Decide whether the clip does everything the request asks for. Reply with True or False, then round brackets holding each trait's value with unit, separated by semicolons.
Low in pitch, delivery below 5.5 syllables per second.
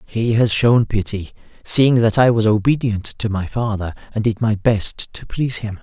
True (110 Hz; 4.6 syllables/s)